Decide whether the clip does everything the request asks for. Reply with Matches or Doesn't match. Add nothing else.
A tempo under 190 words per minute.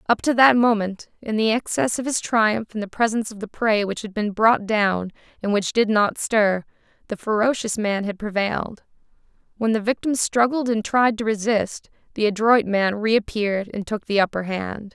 Doesn't match